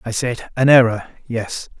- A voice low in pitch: Yes, low, 120 Hz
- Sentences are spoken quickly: No, slow, 135 wpm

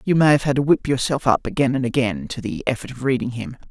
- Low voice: Yes, low, 130 Hz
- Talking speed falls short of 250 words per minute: No, fast, 275 wpm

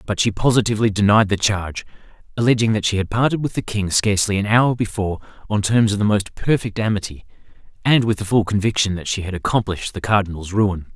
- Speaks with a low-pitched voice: Yes, low, 105 Hz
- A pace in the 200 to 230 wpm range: Yes, fast, 205 wpm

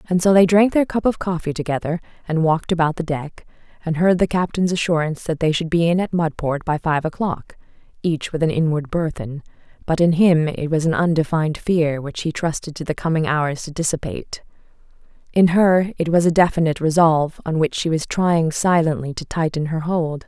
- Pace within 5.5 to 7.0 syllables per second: Yes, 5.6 syllables/s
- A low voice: No, medium, 165 Hz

